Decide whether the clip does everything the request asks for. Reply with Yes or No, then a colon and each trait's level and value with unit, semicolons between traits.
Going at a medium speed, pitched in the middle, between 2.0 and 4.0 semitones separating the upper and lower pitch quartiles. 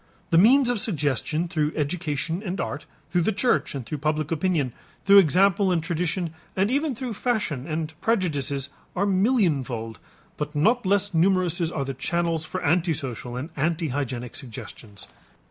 No: average, 150 wpm; medium, 165 Hz; average, 5.0 semitones